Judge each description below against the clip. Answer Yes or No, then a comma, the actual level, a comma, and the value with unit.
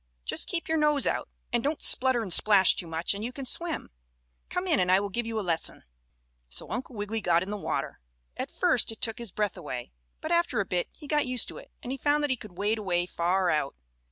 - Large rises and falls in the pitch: Yes, wide, 6.5 semitones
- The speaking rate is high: Yes, fast, 245 wpm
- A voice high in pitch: Yes, high, 220 Hz